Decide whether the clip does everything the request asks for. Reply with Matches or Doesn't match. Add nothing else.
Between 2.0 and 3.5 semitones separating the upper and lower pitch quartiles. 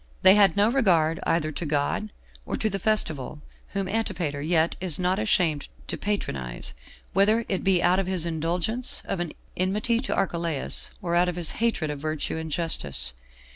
Doesn't match